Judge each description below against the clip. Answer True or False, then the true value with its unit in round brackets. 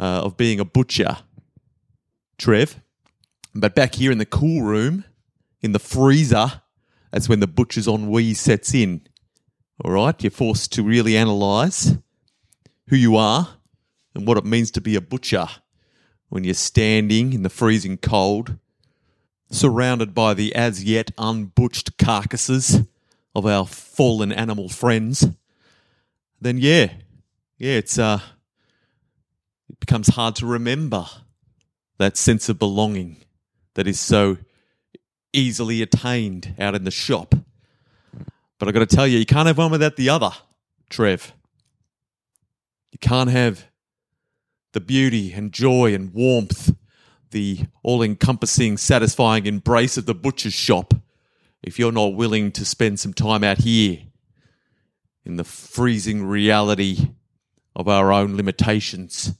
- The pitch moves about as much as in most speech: True (3.3 semitones)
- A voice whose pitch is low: True (115 Hz)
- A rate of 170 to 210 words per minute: False (135 wpm)